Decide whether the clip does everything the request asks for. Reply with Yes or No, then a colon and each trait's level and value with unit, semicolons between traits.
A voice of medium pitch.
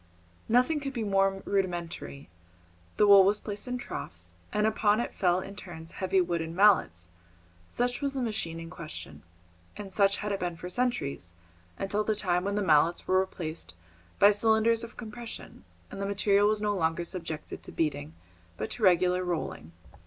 No: high, 195 Hz